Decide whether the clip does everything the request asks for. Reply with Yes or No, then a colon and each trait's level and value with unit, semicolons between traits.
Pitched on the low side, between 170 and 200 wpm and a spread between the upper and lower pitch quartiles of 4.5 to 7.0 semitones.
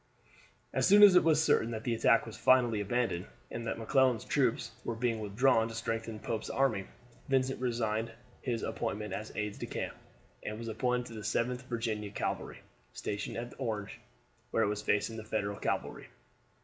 No: low, 115 Hz; average, 175 wpm; narrow, 2.5 semitones